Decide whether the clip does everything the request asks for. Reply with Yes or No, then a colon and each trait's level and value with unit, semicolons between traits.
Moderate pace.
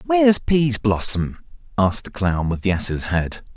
Yes: average, 150 wpm